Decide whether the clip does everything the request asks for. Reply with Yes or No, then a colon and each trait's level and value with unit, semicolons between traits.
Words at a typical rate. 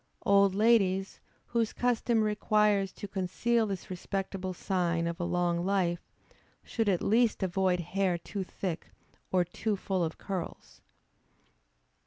No: slow, 130 wpm